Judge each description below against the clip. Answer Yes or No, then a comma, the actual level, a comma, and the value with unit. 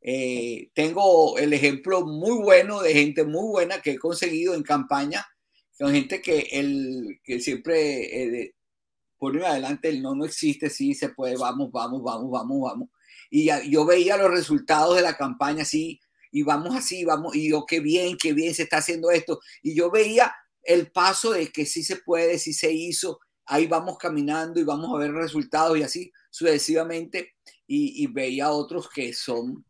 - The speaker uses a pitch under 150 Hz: No, medium, 165 Hz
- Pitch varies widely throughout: No, average, 3.8 semitones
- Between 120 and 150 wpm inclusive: No, average, 180 wpm